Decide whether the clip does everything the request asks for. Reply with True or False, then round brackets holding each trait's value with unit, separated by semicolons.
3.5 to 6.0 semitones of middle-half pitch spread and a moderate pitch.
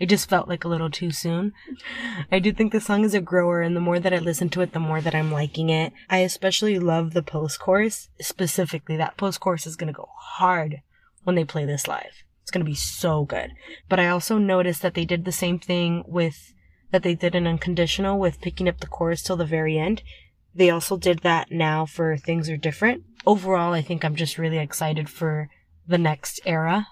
False (2.5 semitones; 175 Hz)